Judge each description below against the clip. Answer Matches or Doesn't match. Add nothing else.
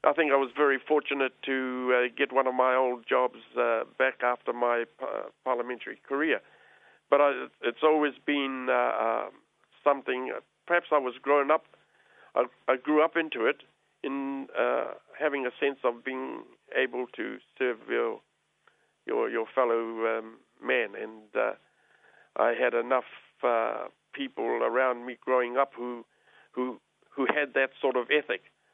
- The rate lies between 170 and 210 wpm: Doesn't match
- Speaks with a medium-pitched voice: Doesn't match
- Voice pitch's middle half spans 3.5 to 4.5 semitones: Doesn't match